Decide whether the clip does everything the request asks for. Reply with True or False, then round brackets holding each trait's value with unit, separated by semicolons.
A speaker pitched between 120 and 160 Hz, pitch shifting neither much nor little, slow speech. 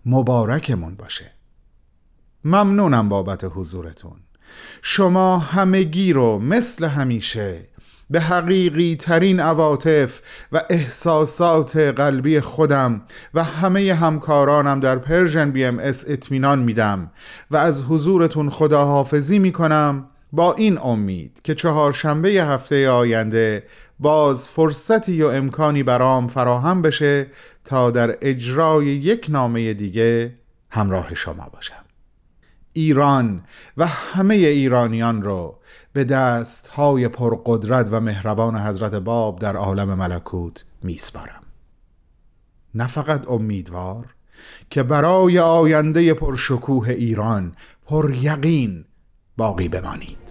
False (135 Hz; 5.8 semitones; 100 wpm)